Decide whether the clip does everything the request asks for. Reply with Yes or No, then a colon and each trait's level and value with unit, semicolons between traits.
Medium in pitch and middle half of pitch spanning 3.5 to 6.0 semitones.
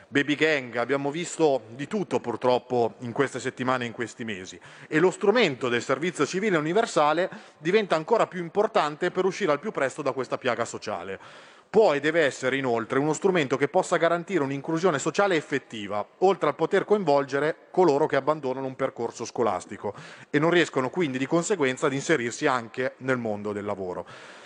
Yes: medium, 145 Hz; average, 5.3 semitones